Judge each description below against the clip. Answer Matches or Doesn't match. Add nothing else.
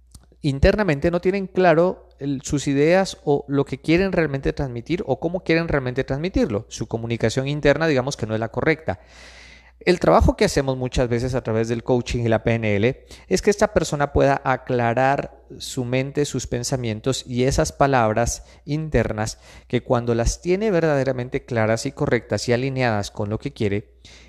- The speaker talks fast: Doesn't match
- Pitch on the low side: Matches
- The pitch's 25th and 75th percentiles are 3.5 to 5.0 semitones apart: Matches